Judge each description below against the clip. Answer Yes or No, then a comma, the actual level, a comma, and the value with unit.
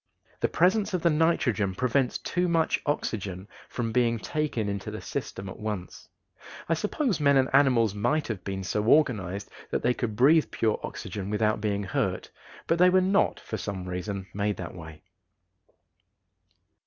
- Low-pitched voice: Yes, low, 115 Hz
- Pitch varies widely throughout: Yes, wide, 7.3 semitones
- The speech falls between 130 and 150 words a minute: No, average, 165 wpm